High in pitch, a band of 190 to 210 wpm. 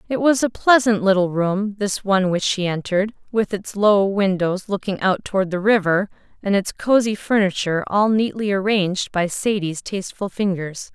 No: high, 200 Hz; average, 170 wpm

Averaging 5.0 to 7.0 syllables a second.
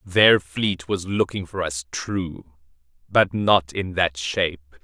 No: 3.5 syllables/s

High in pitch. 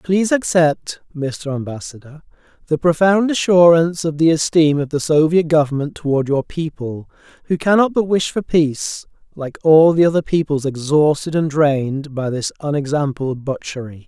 No: medium, 155 Hz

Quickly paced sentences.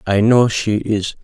No: average, 195 wpm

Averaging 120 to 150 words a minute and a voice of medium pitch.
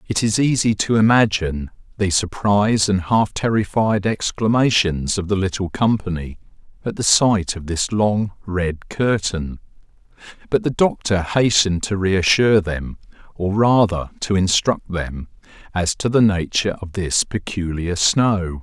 No: average, 140 wpm; low, 100 Hz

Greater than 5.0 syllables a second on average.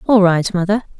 Yes: 5.9 syllables/s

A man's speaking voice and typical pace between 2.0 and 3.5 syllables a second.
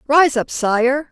No: female; 3.1 syllables/s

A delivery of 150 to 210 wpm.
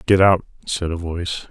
Yes: average, 200 wpm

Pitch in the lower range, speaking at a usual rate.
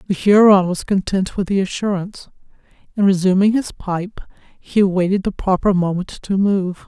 No: high, 190 Hz; average, 155 wpm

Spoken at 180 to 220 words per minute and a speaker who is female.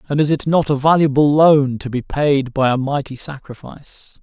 No: average, 200 wpm; male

